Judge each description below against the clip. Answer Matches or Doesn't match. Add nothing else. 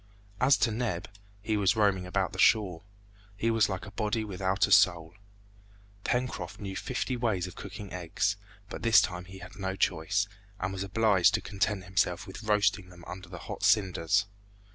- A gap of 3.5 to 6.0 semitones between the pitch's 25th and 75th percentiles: Doesn't match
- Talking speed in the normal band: Matches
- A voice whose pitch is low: Matches